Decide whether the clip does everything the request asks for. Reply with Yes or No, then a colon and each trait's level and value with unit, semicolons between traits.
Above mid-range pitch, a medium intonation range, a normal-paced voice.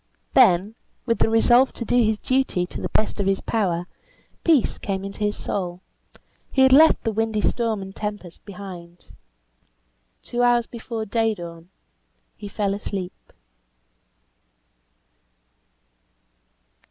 No: high, 210 Hz; average, 3.4 semitones; slow, 130 wpm